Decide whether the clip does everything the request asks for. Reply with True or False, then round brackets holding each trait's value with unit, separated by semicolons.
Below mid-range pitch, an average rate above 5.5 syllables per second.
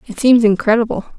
False (225 Hz; 6.1 syllables/s)